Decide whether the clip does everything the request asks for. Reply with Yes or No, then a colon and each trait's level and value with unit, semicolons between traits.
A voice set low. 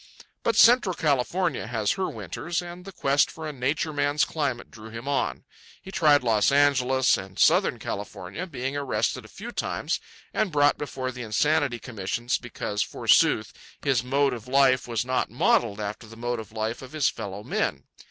Yes: low, 130 Hz